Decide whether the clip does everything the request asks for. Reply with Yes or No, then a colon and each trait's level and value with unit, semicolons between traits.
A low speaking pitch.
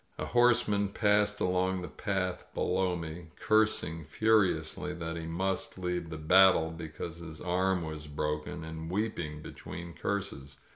Yes: very low, 90 Hz